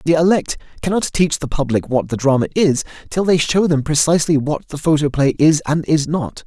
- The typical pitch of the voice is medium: Yes, medium, 155 Hz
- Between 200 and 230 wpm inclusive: Yes, fast, 205 wpm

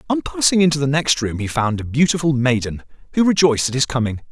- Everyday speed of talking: No, fast, 220 wpm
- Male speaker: Yes, male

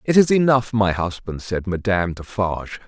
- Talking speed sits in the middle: Yes, average, 165 wpm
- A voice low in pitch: Yes, low, 105 Hz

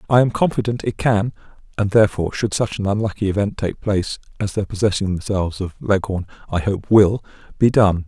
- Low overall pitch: Yes, low, 100 Hz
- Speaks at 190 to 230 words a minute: No, average, 170 wpm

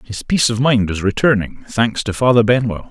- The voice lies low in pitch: Yes, low, 115 Hz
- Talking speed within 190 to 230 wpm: Yes, fast, 205 wpm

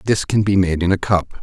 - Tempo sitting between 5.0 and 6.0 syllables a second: Yes, 5.5 syllables/s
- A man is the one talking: Yes, male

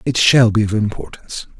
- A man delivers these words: Yes, male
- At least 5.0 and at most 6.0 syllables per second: Yes, 5.8 syllables/s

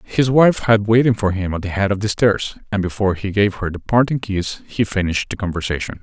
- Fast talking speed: Yes, fast, 240 wpm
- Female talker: No, male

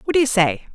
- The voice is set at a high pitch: Yes, high, 220 Hz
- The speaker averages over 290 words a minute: Yes, fast, 325 wpm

